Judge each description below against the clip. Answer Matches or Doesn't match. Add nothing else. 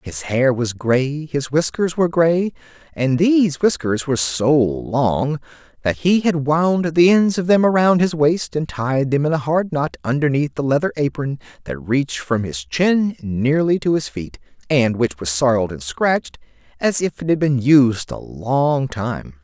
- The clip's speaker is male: Matches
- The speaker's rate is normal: Matches